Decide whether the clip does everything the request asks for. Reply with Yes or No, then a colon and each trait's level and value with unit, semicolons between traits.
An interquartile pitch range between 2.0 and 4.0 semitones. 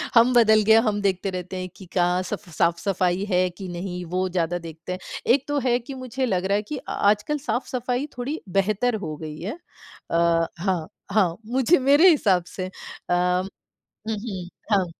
No: average, 4.9 semitones